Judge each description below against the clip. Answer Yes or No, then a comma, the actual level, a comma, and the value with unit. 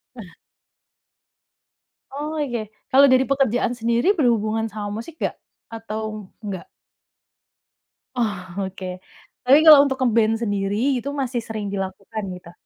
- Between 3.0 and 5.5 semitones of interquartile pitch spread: Yes, average, 4.0 semitones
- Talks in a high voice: Yes, high, 225 Hz